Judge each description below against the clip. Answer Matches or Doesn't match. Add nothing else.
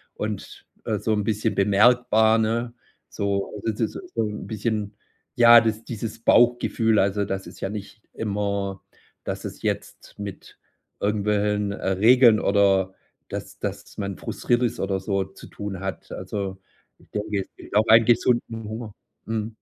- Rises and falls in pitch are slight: Matches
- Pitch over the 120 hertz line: Doesn't match